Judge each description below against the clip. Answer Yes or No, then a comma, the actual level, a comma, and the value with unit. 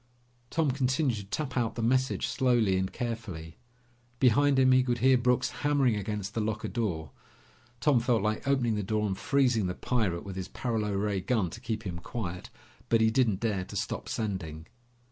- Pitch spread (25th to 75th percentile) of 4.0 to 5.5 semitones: Yes, average, 4.4 semitones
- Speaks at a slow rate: No, average, 185 wpm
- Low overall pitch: Yes, low, 110 Hz